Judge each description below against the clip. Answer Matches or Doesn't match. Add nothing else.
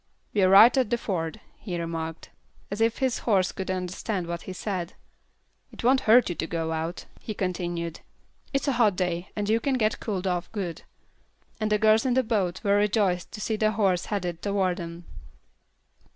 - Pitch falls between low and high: Doesn't match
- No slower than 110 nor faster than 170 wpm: Doesn't match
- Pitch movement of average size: Matches